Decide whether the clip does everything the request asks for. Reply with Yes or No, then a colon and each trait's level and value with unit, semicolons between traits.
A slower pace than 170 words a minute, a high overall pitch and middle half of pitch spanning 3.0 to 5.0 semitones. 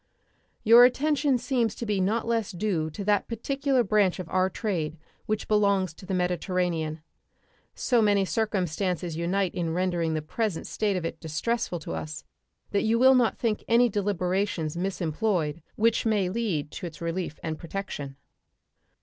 Yes: average, 160 wpm; high, 195 Hz; average, 4.7 semitones